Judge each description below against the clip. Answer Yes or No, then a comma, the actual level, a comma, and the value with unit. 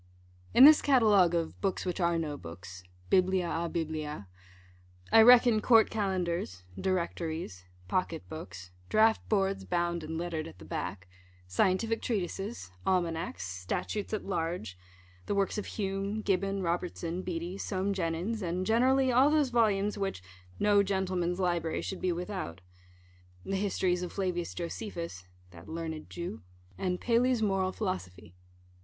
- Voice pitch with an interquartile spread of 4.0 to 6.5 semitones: No, average, 3.6 semitones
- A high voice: No, medium, 180 Hz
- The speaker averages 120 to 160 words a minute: Yes, slow, 135 wpm